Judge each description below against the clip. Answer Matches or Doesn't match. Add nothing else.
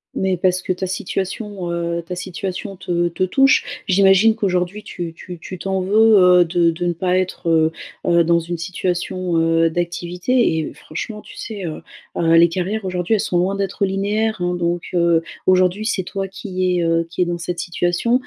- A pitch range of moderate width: Doesn't match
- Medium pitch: Matches